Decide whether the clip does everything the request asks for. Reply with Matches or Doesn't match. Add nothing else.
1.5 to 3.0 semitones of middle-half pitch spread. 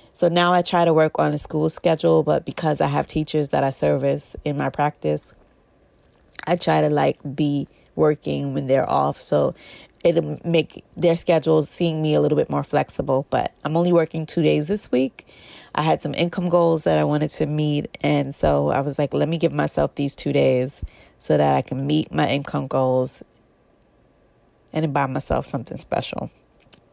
Doesn't match